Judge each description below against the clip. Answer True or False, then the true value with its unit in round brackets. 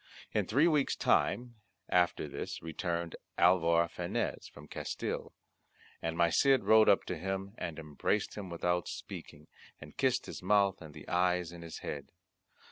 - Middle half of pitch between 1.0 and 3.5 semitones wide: True (3.0 semitones)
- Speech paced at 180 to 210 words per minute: False (155 wpm)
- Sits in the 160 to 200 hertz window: False (90 Hz)